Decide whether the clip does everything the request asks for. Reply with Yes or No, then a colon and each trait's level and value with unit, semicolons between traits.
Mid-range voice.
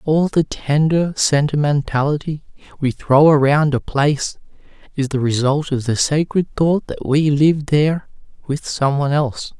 Yes: medium, 145 Hz